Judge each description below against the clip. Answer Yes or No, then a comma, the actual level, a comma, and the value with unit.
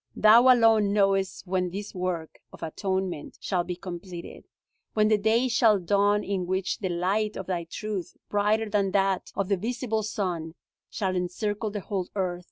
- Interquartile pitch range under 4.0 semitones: Yes, average, 2.8 semitones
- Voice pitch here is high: Yes, high, 195 Hz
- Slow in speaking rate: No, average, 170 wpm